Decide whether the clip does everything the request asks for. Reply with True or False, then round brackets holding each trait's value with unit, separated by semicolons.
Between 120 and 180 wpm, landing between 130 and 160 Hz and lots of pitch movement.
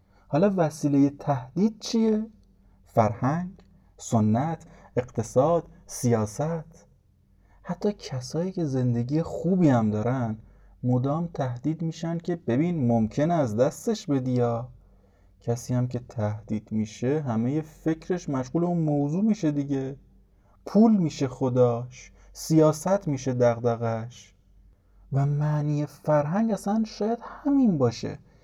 False (105 wpm; 140 Hz; 6.0 semitones)